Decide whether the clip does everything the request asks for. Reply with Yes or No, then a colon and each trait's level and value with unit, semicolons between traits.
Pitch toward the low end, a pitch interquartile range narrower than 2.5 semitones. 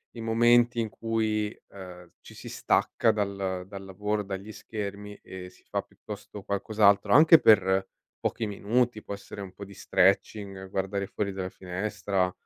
Yes: low, 100 Hz; narrow, 2.0 semitones